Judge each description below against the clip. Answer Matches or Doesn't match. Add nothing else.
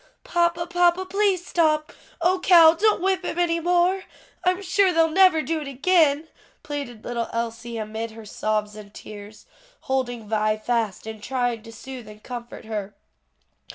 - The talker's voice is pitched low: Doesn't match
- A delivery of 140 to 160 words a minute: Matches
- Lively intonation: Matches